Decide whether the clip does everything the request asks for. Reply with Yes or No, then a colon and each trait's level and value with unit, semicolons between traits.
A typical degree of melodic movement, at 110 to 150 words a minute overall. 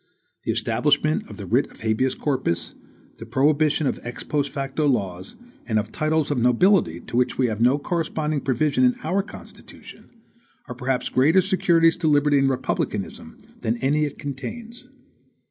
No: average, 3.9 semitones; average, 165 wpm